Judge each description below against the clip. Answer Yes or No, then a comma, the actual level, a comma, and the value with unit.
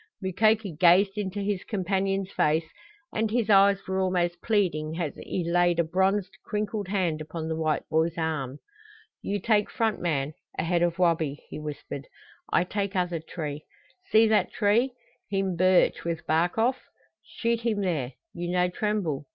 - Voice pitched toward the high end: No, medium, 180 Hz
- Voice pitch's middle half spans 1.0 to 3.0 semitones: No, average, 3.8 semitones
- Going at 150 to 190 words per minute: Yes, average, 160 wpm